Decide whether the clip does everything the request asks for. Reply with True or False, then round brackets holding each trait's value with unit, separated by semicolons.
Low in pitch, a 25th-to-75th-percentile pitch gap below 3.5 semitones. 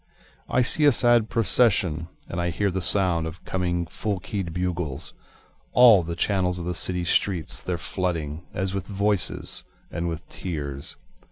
True (90 Hz; 3.0 semitones)